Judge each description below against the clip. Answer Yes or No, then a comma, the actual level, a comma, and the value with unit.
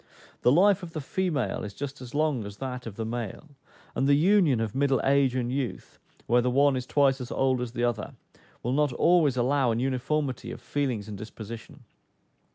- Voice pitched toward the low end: Yes, low, 130 Hz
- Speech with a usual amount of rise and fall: Yes, average, 3.1 semitones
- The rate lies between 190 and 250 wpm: Yes, average, 200 wpm